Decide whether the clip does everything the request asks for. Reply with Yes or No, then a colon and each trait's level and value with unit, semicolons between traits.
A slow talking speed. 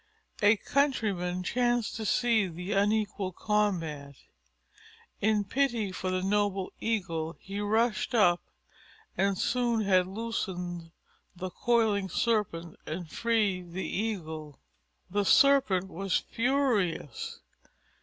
Yes: slow, 105 wpm